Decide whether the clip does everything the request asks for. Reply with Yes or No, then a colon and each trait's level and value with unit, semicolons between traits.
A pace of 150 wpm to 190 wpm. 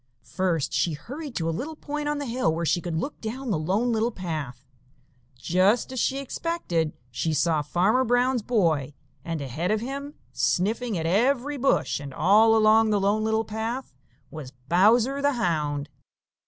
Yes: average, 170 wpm